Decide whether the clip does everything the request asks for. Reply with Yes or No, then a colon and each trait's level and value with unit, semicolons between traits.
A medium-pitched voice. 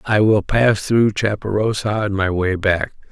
No: low, 105 Hz